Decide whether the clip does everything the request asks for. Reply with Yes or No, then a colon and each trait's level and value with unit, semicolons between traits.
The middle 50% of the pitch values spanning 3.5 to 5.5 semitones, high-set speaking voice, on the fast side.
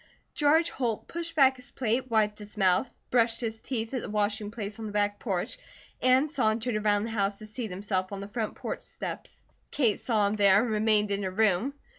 No: average, 3.1 semitones; high, 215 Hz; fast, 210 wpm